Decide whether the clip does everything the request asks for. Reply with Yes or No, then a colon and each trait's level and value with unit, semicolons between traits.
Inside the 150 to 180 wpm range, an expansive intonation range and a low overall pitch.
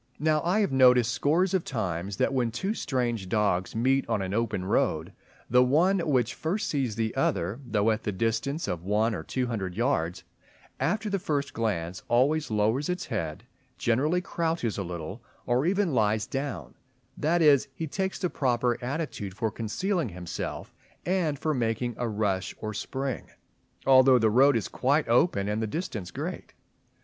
Yes: average, 170 wpm; wide, 6.0 semitones; low, 125 Hz